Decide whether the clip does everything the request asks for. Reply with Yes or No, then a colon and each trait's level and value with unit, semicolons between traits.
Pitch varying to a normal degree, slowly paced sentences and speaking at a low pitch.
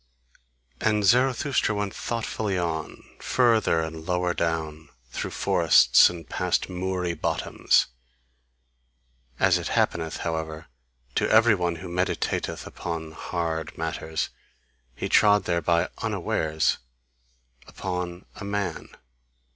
Yes: average, 3.7 semitones; slow, 105 wpm; very low, 90 Hz